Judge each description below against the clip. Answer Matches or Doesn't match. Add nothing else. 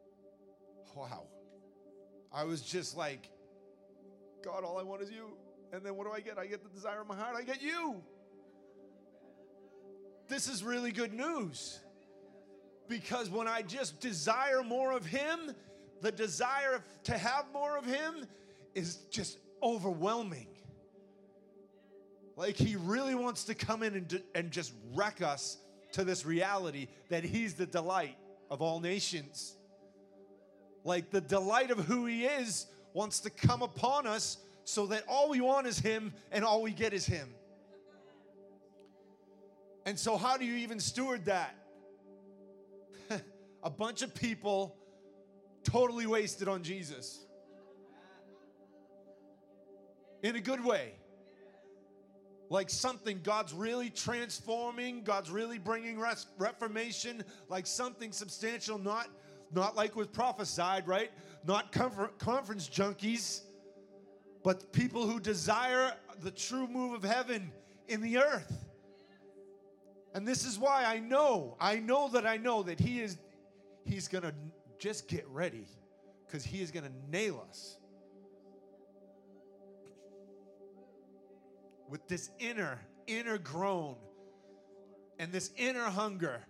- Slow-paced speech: Matches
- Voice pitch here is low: Doesn't match